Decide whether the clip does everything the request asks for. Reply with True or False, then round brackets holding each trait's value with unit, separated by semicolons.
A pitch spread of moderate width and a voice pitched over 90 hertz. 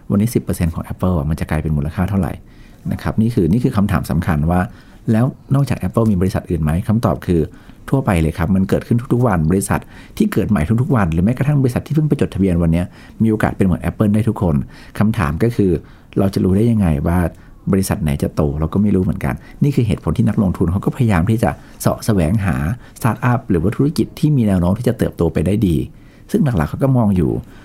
True (5.0 semitones; 100 Hz)